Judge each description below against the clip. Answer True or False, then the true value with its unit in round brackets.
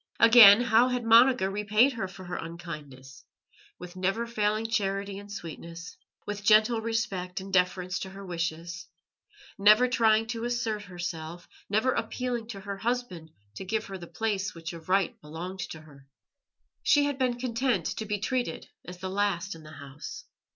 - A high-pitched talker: True (200 Hz)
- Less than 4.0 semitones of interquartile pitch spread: False (4.5 semitones)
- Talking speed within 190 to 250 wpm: False (165 wpm)